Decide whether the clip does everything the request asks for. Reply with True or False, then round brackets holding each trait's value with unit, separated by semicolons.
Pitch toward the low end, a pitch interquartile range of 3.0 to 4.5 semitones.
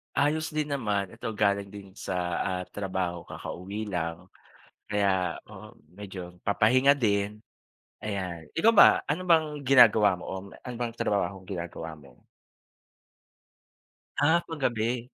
False (105 Hz; 5.5 semitones)